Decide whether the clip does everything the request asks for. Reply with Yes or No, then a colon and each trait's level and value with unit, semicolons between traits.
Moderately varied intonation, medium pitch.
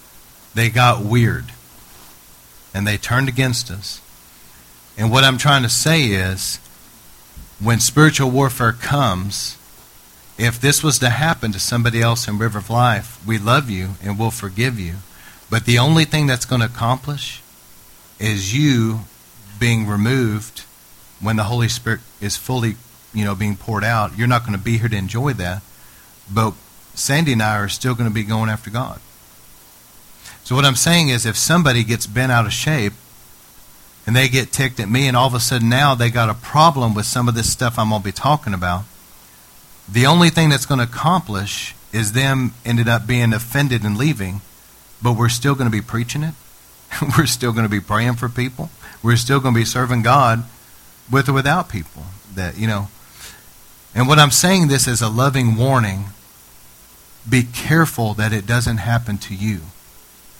No: average, 4.0 semitones; low, 115 Hz